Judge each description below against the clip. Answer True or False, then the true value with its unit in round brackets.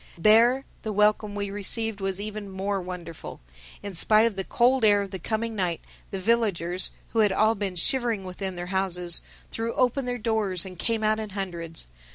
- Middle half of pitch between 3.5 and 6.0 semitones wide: False (3.0 semitones)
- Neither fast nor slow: True (190 wpm)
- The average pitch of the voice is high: True (205 Hz)